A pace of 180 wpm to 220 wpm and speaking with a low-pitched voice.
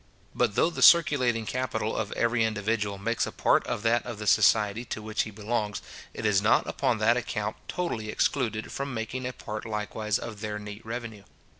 Yes: average, 190 wpm; low, 110 Hz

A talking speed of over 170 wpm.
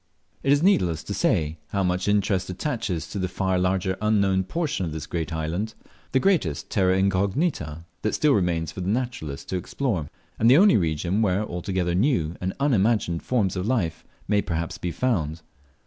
Yes: average, 180 wpm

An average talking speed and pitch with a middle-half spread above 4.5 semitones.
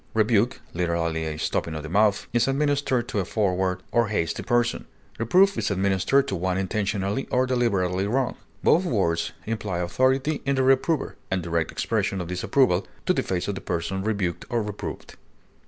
Yes: average, 170 wpm; wide, 5.6 semitones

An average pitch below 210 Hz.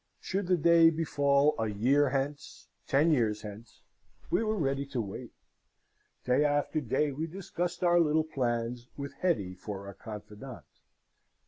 Yes: medium, 140 Hz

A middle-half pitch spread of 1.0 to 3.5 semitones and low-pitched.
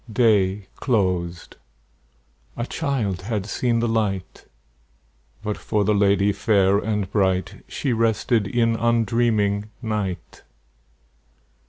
Yes: average, 2.8 semitones; low, 105 Hz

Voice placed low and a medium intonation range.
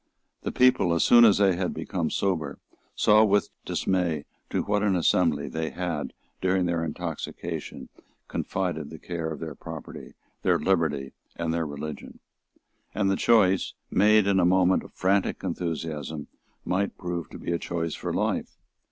Yes: very low, 90 Hz; average, 3.1 semitones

